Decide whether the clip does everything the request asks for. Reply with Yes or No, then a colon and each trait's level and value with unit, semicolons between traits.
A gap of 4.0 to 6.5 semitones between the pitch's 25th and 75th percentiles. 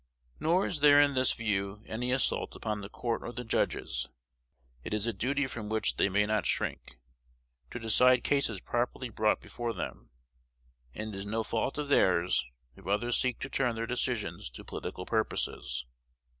No: average, 3.5 semitones